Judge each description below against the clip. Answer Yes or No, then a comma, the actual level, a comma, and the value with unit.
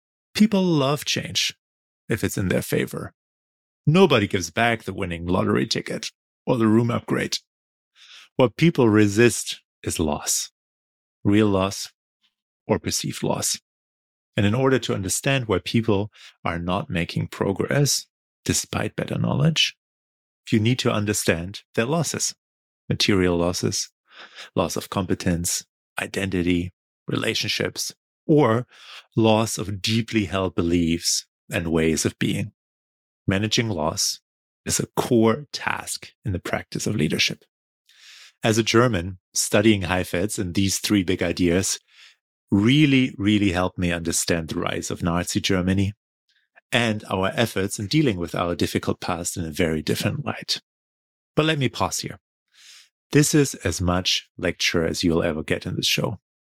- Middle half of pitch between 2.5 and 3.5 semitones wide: No, average, 4.7 semitones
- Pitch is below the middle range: Yes, low, 100 Hz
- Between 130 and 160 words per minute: Yes, slow, 135 wpm